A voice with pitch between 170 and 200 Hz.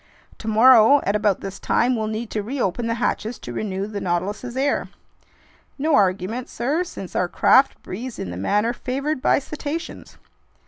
No: high, 225 Hz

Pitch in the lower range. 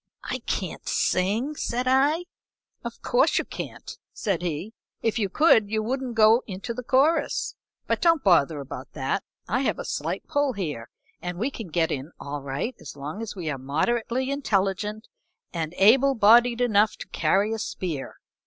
No: high, 215 Hz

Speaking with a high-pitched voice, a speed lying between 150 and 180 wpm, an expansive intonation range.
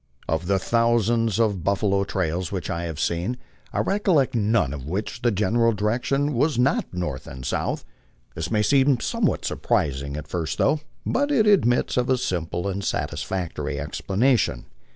No: low, 105 Hz; average, 160 wpm; wide, 5.9 semitones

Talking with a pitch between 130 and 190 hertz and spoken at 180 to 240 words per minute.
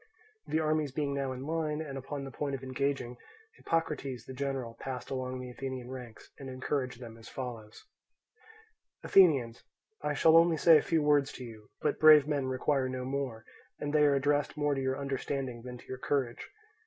Yes: low, 135 Hz; average, 190 wpm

